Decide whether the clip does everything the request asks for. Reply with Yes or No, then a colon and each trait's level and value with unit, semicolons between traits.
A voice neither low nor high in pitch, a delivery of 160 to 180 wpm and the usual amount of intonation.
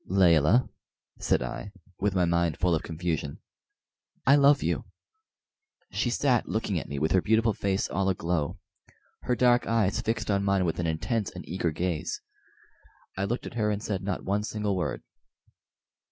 No: very low, 95 Hz; average, 170 wpm; average, 4.3 semitones